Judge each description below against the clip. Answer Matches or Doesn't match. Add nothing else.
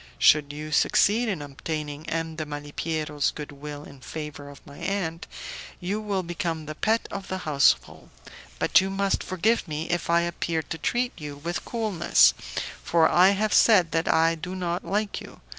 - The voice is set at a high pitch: Doesn't match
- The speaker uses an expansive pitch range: Doesn't match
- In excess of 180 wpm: Doesn't match